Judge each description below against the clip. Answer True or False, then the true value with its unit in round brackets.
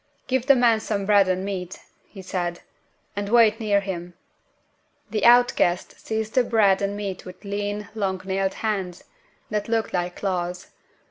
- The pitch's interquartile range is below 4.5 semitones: True (2.8 semitones)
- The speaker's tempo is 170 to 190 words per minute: False (160 wpm)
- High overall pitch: True (200 Hz)